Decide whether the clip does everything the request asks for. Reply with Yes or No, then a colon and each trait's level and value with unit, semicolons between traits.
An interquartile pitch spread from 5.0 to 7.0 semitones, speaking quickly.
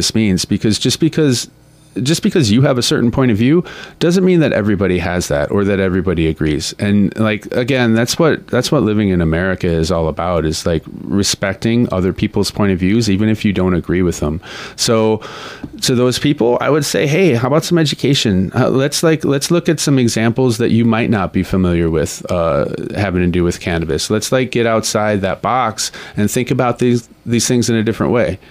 Yes: average, 5.3 semitones; fast, 210 wpm